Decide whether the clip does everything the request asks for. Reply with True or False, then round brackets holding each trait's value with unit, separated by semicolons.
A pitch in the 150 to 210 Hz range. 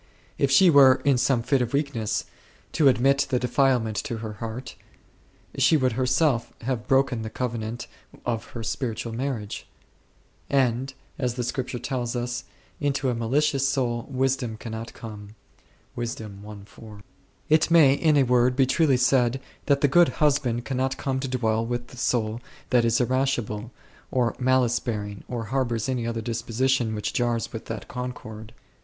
False (125 Hz)